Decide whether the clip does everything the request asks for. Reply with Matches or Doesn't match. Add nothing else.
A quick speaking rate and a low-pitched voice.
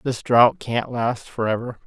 Doesn't match